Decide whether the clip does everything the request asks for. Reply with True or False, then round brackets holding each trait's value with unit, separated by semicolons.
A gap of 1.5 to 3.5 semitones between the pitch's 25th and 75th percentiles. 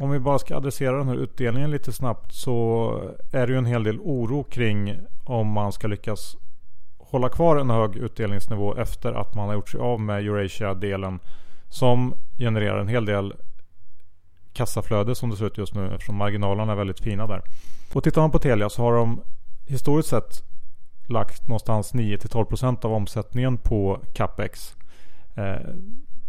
False (3.9 semitones)